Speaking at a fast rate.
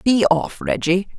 No: average, 150 wpm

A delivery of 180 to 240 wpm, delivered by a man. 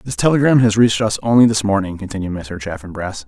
Yes: average, 200 wpm; male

